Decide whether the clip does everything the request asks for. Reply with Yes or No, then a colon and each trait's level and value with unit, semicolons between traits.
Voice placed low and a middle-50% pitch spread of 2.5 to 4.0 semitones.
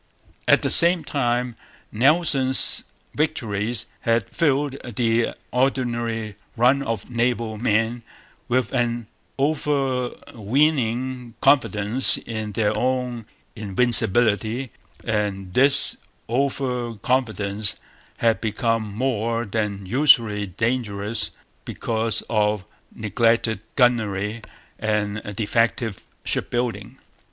Yes: low, 115 Hz; average, 2.9 semitones